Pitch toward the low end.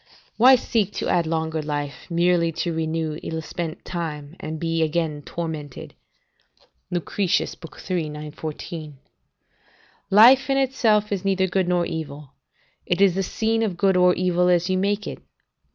No: medium, 175 Hz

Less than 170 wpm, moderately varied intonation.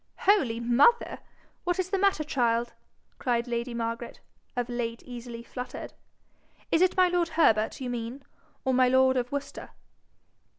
Yes: average, 145 wpm; average, 4.9 semitones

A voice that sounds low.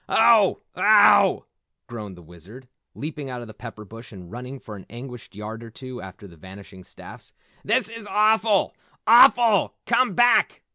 Yes: low, 120 Hz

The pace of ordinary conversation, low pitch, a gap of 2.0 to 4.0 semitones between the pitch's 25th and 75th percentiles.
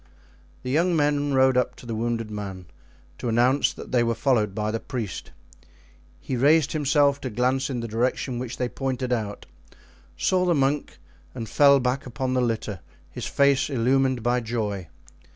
Yes: average, 170 wpm; low, 125 Hz; average, 3.2 semitones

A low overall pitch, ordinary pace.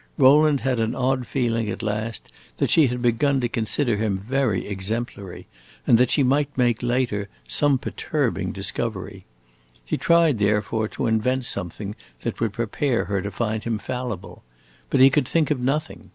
Yes: low, 120 Hz; average, 165 wpm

